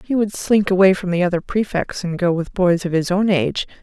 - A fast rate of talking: Yes, fast, 250 wpm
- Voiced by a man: No, female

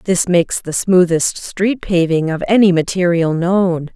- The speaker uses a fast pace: No, average, 150 wpm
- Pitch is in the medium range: Yes, medium, 180 Hz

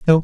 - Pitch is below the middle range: No, medium, 160 Hz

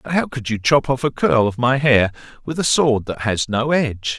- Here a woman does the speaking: No, male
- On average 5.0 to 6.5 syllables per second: Yes, 5.1 syllables/s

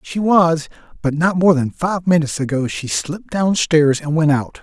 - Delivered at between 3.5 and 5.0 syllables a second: Yes, 4.8 syllables/s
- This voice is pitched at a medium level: Yes, medium, 155 Hz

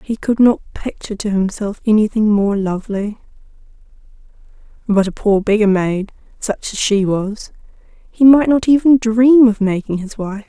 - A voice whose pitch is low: No, high, 215 Hz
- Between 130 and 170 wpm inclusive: Yes, average, 155 wpm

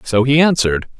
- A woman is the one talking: No, male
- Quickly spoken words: No, average, 180 wpm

